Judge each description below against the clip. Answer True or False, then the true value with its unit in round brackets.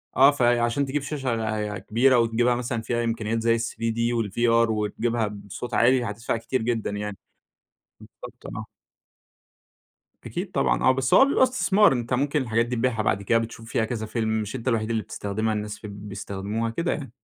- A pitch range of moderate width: False (2.3 semitones)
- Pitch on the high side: False (115 Hz)